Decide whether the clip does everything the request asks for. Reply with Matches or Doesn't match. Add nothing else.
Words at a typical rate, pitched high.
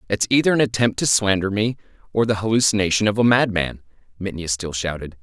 Doesn't match